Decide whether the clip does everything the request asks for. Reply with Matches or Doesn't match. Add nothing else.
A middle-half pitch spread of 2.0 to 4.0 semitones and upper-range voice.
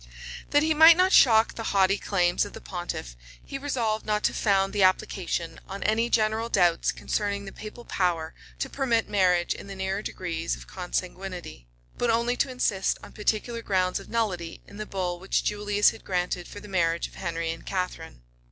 Matches